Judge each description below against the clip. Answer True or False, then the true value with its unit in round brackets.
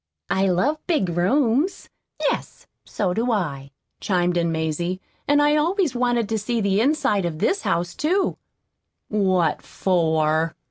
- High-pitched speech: True (195 Hz)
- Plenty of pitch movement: True (7.5 semitones)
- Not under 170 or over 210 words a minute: False (140 wpm)